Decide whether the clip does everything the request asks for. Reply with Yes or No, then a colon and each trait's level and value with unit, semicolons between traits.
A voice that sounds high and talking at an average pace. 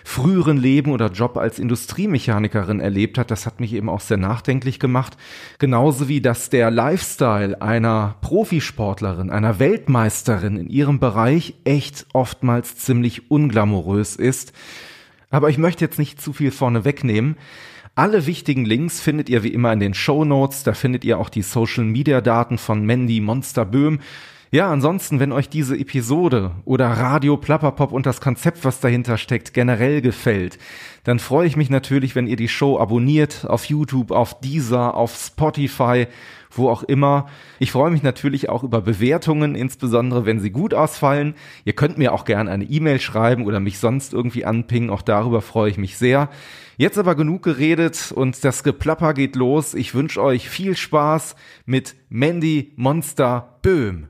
No: low, 130 Hz; average, 165 wpm